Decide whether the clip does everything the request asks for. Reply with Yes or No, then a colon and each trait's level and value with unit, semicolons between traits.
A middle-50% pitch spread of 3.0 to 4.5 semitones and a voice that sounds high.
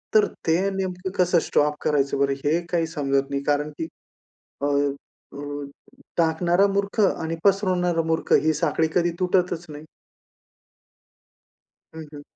No: average, 3.5 semitones; medium, 165 Hz